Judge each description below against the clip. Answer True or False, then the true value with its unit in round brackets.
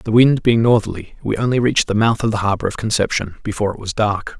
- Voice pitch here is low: True (110 Hz)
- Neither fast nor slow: False (245 wpm)